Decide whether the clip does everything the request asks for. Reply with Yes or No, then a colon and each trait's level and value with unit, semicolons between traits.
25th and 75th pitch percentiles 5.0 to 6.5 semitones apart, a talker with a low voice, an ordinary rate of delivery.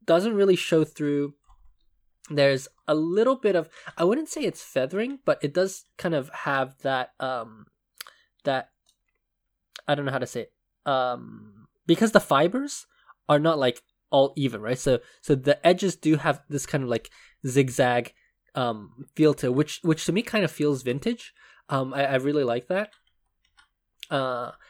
No: average, 5.3 semitones; medium, 145 Hz; average, 170 wpm